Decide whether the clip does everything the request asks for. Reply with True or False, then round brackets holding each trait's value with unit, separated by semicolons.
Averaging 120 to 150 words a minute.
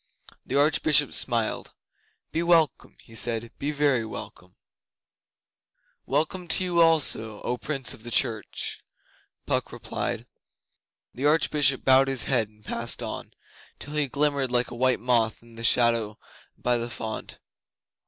True (140 wpm)